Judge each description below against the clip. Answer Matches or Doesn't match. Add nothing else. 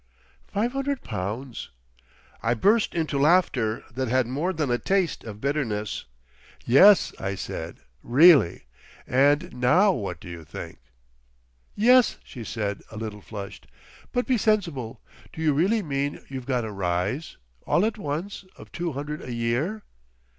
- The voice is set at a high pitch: Doesn't match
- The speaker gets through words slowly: Doesn't match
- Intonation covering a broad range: Matches